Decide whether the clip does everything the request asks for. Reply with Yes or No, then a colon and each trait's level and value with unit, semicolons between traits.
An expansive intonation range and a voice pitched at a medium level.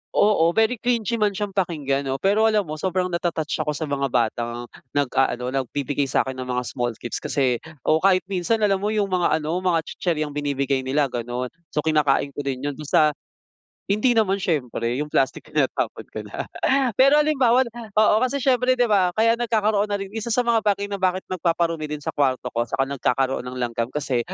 Yes: wide, 7.5 semitones; medium, 165 Hz